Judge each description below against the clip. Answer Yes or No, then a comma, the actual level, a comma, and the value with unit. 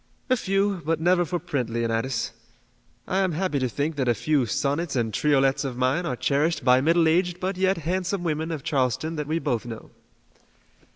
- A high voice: No, medium, 150 Hz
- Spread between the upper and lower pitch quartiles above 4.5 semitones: Yes, average, 5.2 semitones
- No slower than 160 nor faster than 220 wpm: Yes, average, 190 wpm